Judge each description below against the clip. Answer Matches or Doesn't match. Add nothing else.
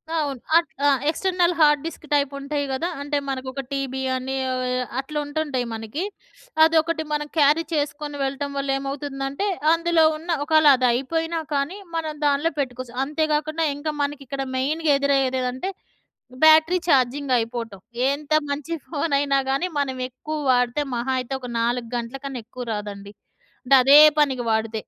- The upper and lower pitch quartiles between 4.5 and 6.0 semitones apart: Doesn't match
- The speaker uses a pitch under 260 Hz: Doesn't match